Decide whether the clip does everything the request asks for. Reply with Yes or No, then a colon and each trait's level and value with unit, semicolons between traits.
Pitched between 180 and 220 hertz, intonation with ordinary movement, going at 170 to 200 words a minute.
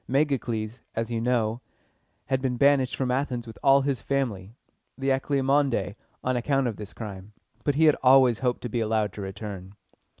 No: low, 125 Hz; average, 3.8 semitones; average, 175 wpm